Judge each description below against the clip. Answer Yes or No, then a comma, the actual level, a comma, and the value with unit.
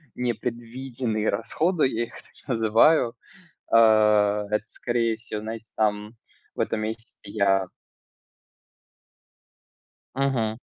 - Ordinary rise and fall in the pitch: No, narrow, 2.0 semitones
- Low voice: Yes, low, 115 Hz